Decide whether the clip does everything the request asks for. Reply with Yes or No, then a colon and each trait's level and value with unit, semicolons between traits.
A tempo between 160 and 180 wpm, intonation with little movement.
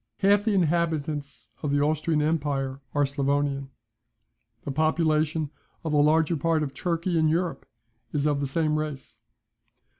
No: average, 145 wpm; narrow, 2.3 semitones